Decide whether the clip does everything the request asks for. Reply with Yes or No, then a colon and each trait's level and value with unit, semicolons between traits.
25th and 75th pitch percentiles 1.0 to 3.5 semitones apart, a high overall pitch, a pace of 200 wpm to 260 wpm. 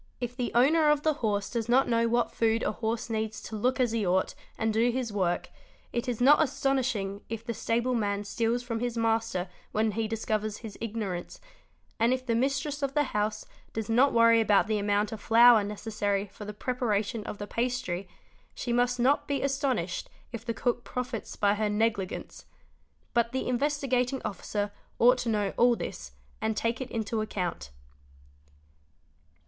No: average, 2.8 semitones; high, 230 Hz; average, 180 wpm